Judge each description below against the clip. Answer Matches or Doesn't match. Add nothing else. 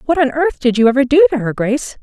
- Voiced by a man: Doesn't match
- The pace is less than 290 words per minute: Doesn't match